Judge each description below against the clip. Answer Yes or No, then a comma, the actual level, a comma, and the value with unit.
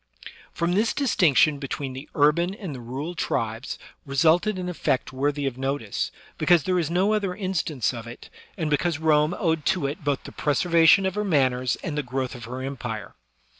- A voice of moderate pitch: Yes, medium, 150 Hz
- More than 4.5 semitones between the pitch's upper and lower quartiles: Yes, average, 5.1 semitones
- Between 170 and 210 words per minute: Yes, average, 185 wpm